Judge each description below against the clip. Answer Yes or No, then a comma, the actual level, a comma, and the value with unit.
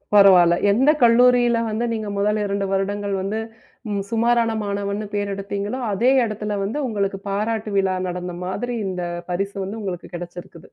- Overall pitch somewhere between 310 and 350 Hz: No, high, 200 Hz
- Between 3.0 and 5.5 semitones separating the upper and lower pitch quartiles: No, narrow, 2.5 semitones